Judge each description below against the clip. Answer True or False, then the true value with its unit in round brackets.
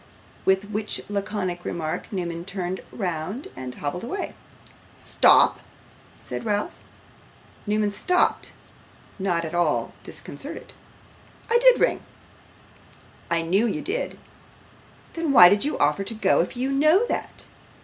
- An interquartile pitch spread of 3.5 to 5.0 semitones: False (5.5 semitones)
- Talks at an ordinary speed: False (125 wpm)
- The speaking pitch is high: True (200 Hz)